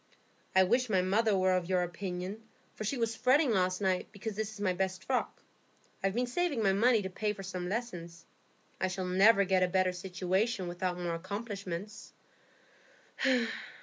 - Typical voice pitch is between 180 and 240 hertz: Yes, high, 190 Hz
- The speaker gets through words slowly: No, average, 175 wpm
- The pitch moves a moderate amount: Yes, average, 3.0 semitones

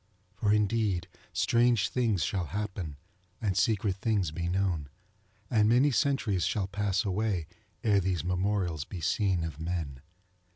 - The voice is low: Yes, very low, 95 Hz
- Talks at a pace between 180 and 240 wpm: No, slow, 135 wpm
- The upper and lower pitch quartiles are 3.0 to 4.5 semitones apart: Yes, average, 3.3 semitones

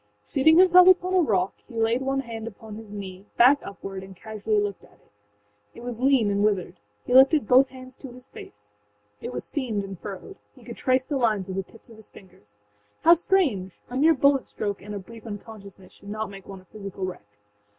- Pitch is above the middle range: Yes, high, 220 Hz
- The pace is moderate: No, fast, 215 wpm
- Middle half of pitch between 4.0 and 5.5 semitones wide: Yes, average, 5.1 semitones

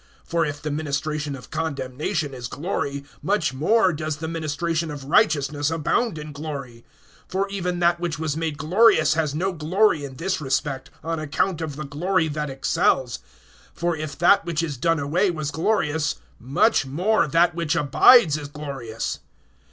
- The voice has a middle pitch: Yes, medium, 155 Hz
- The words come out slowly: No, average, 165 wpm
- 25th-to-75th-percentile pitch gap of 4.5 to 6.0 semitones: No, average, 3.0 semitones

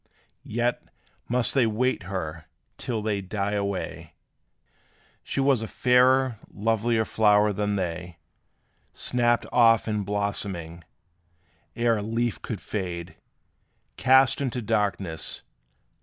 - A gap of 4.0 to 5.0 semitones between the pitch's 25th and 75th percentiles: No, average, 3.4 semitones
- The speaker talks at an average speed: No, slow, 110 wpm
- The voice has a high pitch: No, low, 105 Hz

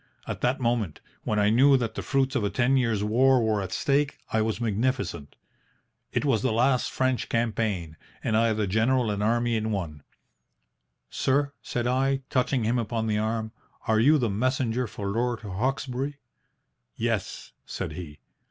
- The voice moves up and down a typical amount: Yes, average, 3.3 semitones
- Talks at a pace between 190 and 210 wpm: No, average, 170 wpm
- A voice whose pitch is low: Yes, low, 115 Hz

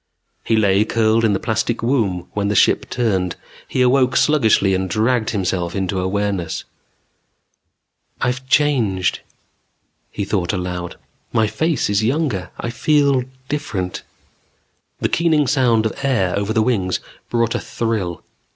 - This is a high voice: No, low, 110 Hz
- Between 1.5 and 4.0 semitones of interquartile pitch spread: No, average, 4.8 semitones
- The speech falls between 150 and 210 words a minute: No, slow, 135 wpm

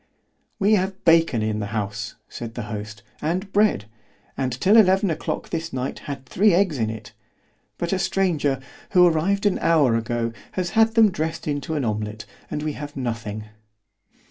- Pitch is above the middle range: No, medium, 150 Hz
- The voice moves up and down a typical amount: No, wide, 8.6 semitones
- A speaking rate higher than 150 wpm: Yes, average, 165 wpm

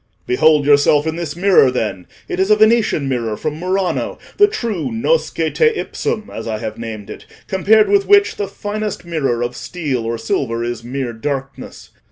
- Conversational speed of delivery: Yes, average, 175 wpm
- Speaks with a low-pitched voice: No, medium, 150 Hz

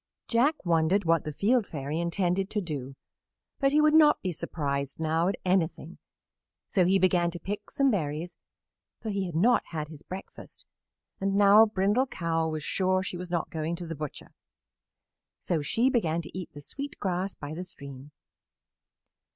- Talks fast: No, average, 175 wpm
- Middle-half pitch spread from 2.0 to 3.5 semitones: No, average, 4.0 semitones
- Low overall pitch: No, medium, 180 Hz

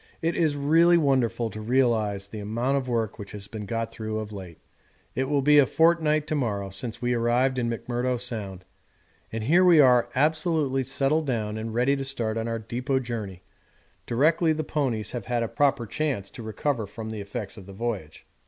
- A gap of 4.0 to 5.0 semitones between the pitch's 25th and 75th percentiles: Yes, average, 4.3 semitones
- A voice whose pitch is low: Yes, low, 120 Hz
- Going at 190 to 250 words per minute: Yes, average, 200 wpm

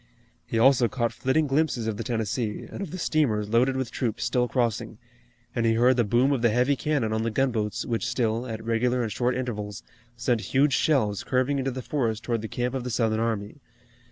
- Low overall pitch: Yes, low, 120 Hz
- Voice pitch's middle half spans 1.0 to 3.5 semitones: Yes, narrow, 2.6 semitones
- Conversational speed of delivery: No, fast, 215 wpm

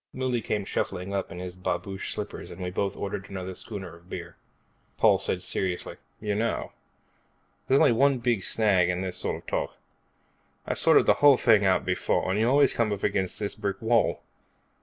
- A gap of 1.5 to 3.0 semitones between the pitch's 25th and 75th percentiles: No, average, 3.6 semitones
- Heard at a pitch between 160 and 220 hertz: No, low, 100 Hz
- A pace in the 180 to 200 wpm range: Yes, average, 190 wpm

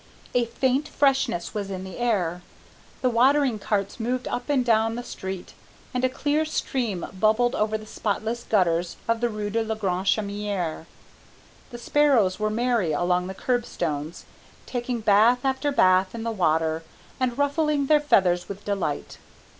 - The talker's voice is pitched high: Yes, high, 220 Hz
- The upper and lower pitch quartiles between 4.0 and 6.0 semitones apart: Yes, average, 4.7 semitones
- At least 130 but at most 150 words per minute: No, average, 160 wpm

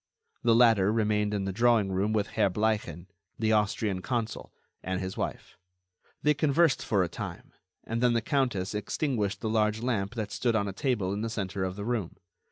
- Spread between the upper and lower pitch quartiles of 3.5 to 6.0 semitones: No, average, 3.0 semitones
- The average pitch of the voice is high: No, low, 105 Hz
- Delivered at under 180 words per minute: No, average, 190 wpm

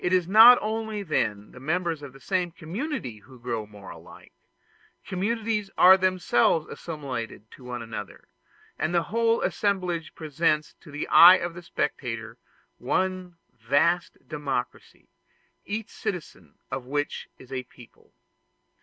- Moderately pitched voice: Yes, medium, 165 Hz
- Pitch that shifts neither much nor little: No, wide, 6.8 semitones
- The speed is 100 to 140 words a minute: Yes, slow, 135 wpm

